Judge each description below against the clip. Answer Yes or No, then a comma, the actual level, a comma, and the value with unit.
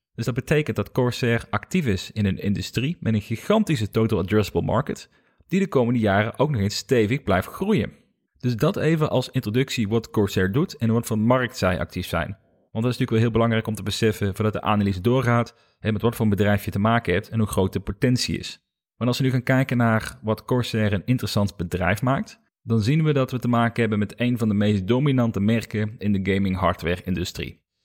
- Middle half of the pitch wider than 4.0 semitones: No, average, 3.4 semitones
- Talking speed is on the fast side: Yes, fast, 220 wpm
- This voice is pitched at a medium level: No, low, 110 Hz